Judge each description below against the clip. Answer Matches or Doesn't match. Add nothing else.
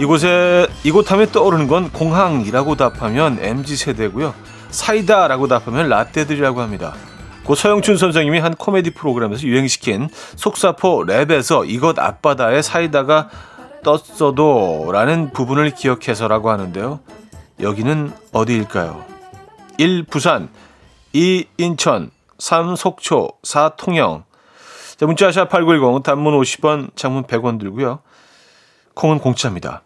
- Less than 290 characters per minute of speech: Matches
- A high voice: Doesn't match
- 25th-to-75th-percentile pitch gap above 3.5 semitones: Matches